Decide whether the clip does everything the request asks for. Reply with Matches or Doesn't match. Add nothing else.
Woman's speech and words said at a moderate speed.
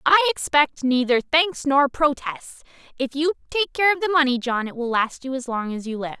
Doesn't match